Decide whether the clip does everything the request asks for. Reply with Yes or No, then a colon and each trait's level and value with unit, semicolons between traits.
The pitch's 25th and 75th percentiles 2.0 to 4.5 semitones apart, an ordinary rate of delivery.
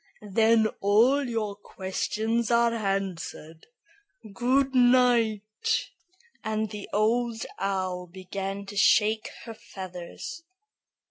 No: average, 3.2 semitones; slow, 90 wpm